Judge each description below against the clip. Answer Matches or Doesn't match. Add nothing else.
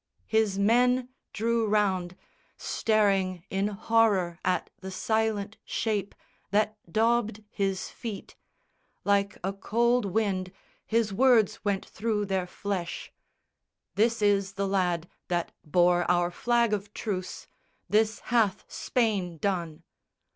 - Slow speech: Matches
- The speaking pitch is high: Matches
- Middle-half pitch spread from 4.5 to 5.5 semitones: Doesn't match